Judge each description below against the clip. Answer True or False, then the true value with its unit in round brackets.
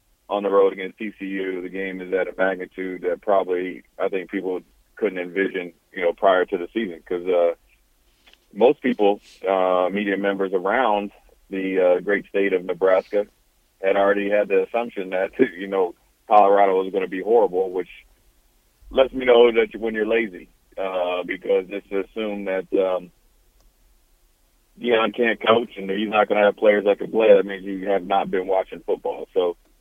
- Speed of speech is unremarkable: True (180 wpm)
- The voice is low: True (100 Hz)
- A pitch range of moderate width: True (3.2 semitones)